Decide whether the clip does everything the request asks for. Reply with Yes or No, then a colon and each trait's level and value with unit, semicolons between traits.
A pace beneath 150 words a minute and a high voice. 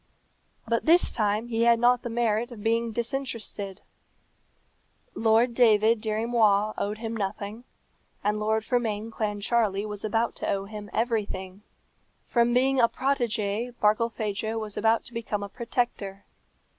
Yes: average, 140 wpm; high, 225 Hz